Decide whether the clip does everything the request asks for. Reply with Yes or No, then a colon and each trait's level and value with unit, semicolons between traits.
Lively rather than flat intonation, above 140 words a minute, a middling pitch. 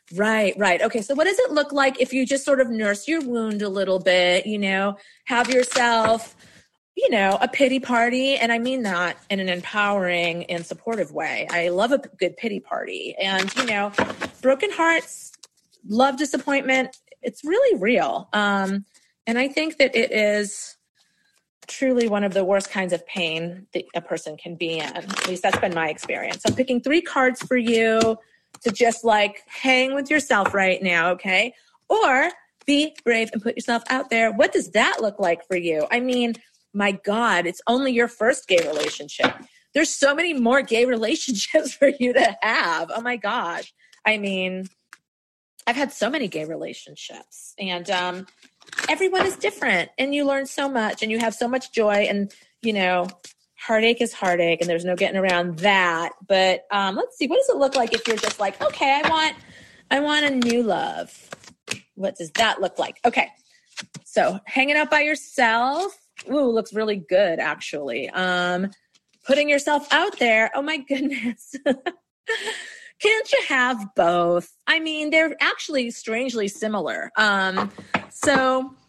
No: wide, 5.9 semitones; average, 175 wpm; high, 230 Hz